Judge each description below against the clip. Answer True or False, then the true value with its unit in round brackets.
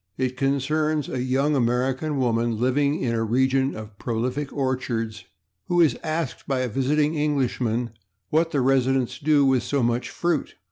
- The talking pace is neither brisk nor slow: True (155 wpm)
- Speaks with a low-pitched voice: True (130 Hz)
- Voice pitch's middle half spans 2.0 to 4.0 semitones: True (3.0 semitones)